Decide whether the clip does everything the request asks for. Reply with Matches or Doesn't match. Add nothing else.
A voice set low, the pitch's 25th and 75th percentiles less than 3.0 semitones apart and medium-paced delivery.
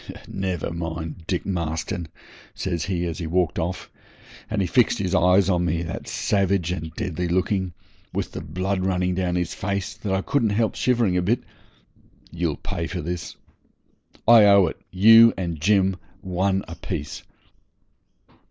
Matches